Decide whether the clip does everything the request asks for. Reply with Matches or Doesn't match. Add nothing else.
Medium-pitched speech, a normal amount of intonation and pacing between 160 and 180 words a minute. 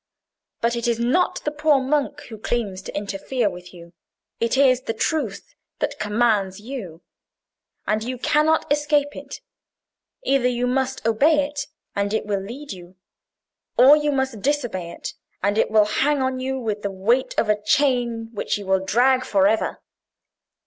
Doesn't match